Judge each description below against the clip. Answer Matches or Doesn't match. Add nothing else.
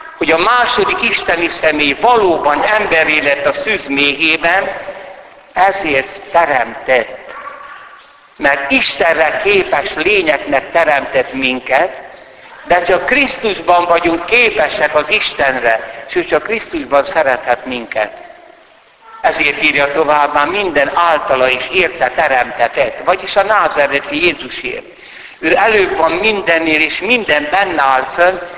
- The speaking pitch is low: Doesn't match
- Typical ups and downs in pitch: Doesn't match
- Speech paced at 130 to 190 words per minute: Doesn't match